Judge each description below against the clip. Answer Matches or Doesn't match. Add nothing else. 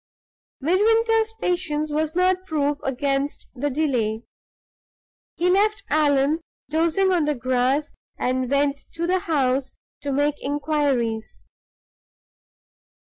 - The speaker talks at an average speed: Doesn't match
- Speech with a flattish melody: Doesn't match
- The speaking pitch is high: Matches